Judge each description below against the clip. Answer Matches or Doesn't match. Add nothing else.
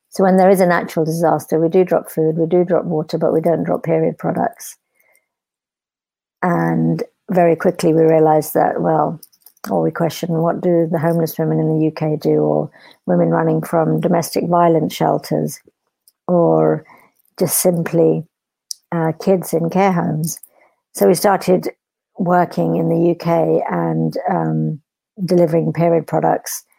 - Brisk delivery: Doesn't match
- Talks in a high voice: Doesn't match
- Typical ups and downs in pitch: Doesn't match